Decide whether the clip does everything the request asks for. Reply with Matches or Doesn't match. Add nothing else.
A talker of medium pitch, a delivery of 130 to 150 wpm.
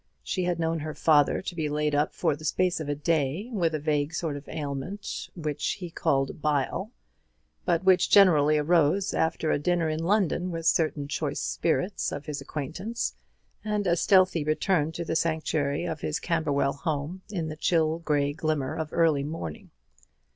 Doesn't match